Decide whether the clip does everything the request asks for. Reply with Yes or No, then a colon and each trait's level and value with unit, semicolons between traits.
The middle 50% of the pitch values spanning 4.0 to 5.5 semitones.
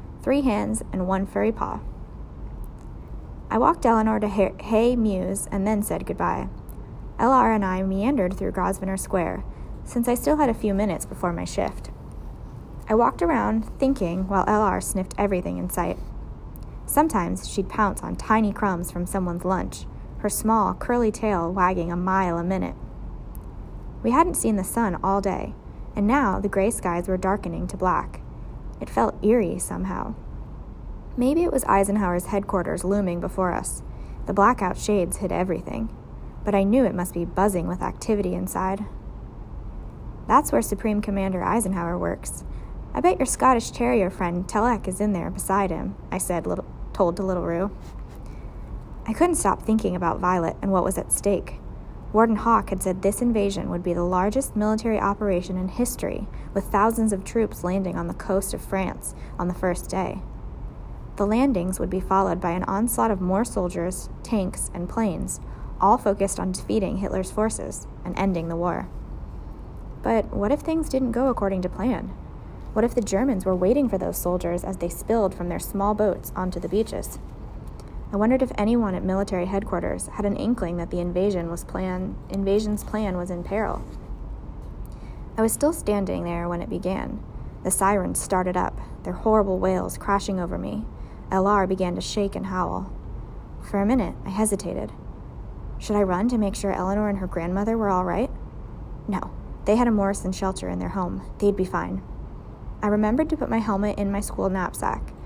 No: average, 3.0 semitones